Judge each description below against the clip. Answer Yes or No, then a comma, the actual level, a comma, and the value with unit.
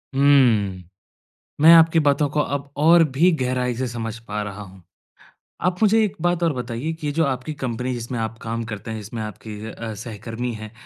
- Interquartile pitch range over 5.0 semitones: Yes, wide, 5.5 semitones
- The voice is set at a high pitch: No, low, 125 Hz